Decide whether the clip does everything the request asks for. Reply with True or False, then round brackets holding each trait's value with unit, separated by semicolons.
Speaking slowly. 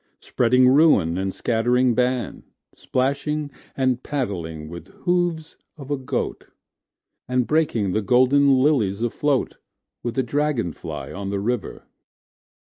True (110 wpm)